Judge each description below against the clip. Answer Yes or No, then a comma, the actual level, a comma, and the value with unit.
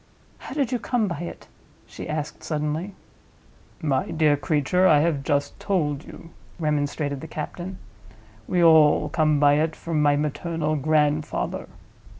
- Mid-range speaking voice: Yes, medium, 155 Hz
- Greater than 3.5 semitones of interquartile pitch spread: No, narrow, 2.5 semitones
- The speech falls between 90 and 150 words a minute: Yes, average, 145 wpm